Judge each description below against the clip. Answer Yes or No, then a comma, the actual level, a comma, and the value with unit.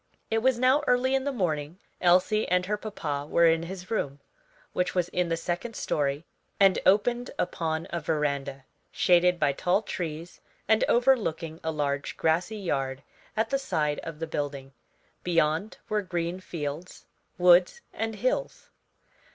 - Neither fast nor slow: Yes, average, 150 wpm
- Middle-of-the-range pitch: Yes, medium, 175 Hz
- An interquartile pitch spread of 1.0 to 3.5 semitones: No, wide, 5.5 semitones